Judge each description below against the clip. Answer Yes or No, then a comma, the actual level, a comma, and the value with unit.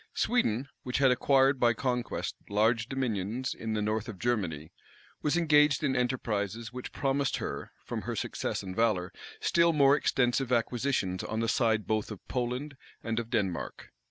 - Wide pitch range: No, average, 3.7 semitones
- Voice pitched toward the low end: Yes, low, 120 Hz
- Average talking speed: Yes, average, 160 wpm